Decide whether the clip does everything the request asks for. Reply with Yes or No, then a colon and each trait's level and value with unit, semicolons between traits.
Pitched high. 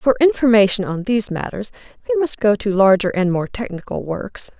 Yes: high, 220 Hz